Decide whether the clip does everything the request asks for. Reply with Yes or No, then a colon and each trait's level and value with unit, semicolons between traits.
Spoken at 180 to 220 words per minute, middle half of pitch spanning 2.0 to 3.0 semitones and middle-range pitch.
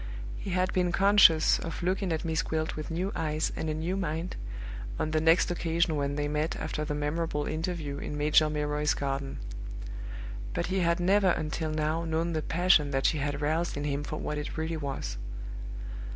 Yes: average, 190 wpm; narrow, 2.4 semitones; medium, 155 Hz